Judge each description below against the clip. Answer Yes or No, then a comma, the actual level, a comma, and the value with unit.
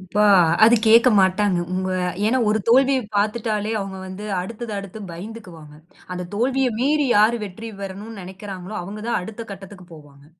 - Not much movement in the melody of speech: No, average, 3.4 semitones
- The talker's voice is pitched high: Yes, high, 205 Hz